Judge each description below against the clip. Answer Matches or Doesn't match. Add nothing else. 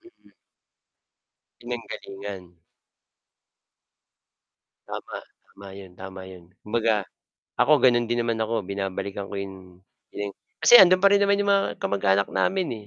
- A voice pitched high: Doesn't match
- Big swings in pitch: Doesn't match